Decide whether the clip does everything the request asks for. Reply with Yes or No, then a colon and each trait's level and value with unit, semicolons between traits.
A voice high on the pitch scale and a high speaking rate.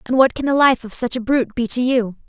Yes: very high, 250 Hz; fast, 315 wpm